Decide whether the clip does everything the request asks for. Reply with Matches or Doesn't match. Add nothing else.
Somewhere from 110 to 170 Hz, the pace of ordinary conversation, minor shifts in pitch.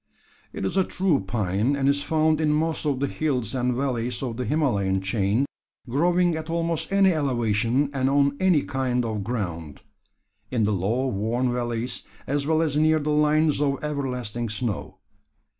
Doesn't match